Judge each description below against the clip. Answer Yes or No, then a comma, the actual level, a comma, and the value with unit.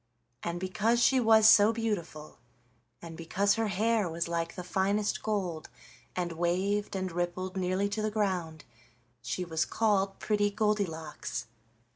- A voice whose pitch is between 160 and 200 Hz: Yes, high, 190 Hz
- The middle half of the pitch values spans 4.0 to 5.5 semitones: No, average, 3.6 semitones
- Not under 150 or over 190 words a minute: No, average, 140 wpm